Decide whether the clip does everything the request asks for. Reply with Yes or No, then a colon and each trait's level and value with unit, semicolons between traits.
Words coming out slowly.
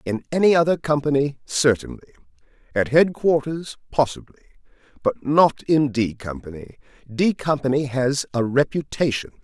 Yes: slow, 115 wpm